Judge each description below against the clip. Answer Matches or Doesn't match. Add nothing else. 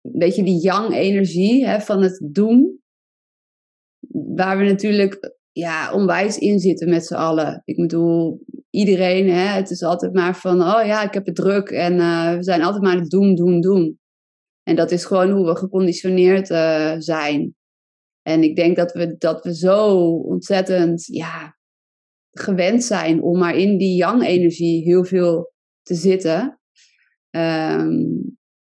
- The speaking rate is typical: Matches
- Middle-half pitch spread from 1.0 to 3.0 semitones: Matches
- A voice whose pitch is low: Doesn't match